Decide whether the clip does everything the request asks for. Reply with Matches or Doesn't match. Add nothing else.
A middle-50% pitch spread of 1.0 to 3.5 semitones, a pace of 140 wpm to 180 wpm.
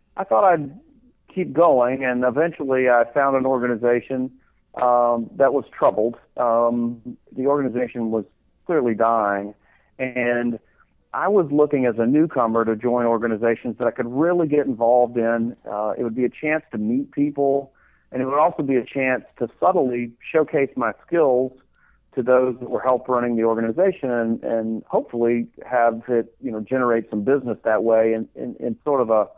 Matches